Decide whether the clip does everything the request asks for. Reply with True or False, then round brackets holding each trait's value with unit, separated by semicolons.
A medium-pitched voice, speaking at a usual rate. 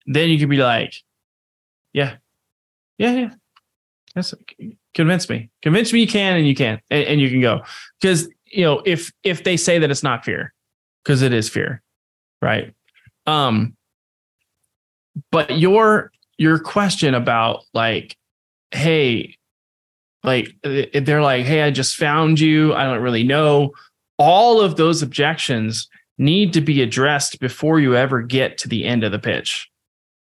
True (145 Hz; 150 wpm)